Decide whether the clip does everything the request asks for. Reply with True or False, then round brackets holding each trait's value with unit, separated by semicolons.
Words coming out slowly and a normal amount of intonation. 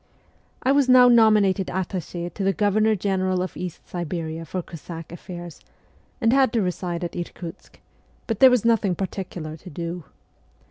False (160 wpm; 3.9 semitones)